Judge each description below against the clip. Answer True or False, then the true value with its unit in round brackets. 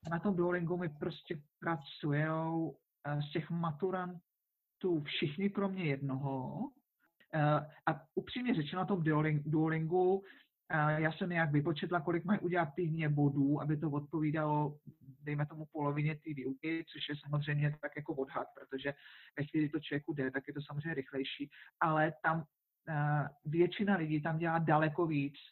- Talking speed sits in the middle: True (140 wpm)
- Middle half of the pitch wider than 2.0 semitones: True (2.6 semitones)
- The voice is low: False (155 Hz)